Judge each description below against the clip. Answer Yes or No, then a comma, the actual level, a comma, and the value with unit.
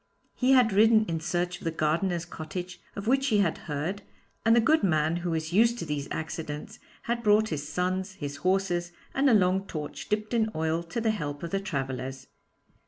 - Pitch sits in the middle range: Yes, medium, 180 Hz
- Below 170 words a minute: No, average, 200 wpm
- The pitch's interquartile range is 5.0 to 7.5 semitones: Yes, average, 5.3 semitones